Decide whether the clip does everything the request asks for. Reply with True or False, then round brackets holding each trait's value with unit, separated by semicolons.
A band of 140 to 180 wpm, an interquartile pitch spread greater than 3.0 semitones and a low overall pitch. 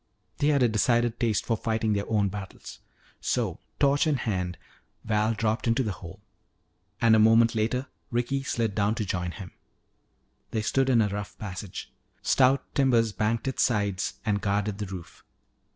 False (170 wpm; 2.7 semitones; 110 Hz)